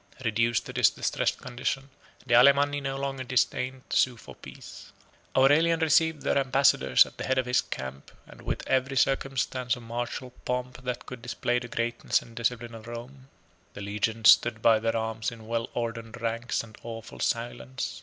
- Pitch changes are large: No, narrow, 2.4 semitones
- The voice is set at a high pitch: No, low, 120 Hz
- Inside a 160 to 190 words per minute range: Yes, average, 175 wpm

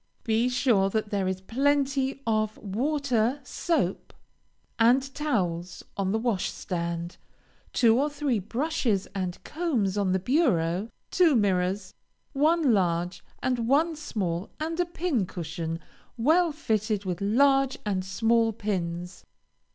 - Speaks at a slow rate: Yes, slow, 125 wpm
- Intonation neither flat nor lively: No, wide, 6.5 semitones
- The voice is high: Yes, high, 225 Hz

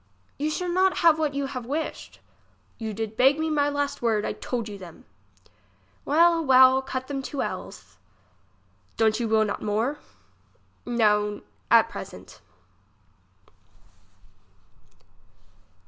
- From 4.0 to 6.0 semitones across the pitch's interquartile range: Yes, average, 5.0 semitones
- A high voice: Yes, very high, 260 Hz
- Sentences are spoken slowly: Yes, slow, 125 wpm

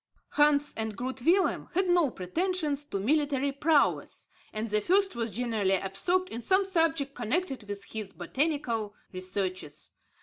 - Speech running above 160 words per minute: No, average, 140 wpm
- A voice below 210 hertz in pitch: No, very high, 270 Hz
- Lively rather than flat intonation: Yes, wide, 7.5 semitones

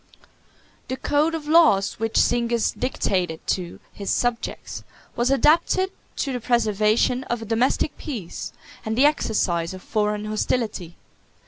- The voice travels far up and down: No, average, 4.0 semitones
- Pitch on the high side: Yes, high, 230 Hz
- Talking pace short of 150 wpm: Yes, slow, 135 wpm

